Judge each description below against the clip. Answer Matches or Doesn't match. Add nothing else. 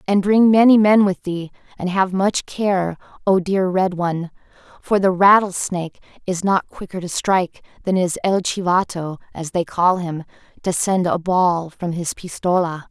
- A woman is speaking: Matches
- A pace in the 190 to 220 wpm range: Doesn't match